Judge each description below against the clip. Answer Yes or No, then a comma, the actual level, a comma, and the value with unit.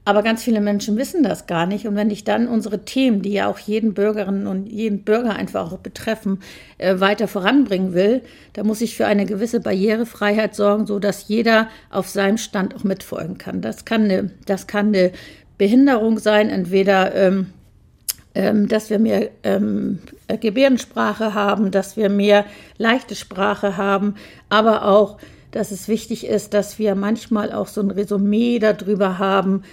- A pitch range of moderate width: No, narrow, 1.8 semitones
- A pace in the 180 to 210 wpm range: No, average, 165 wpm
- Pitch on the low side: No, high, 210 Hz